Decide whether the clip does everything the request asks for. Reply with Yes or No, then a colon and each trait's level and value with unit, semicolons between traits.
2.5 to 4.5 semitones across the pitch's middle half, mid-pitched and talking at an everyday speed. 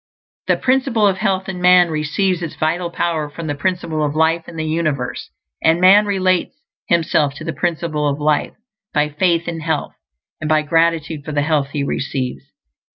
Yes: average, 3.0 semitones; medium, 160 Hz; average, 180 wpm